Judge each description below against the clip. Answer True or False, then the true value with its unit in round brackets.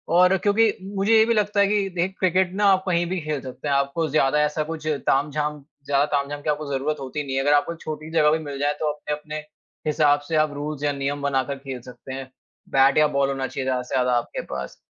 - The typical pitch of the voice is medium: True (150 Hz)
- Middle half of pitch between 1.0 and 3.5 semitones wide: True (3.0 semitones)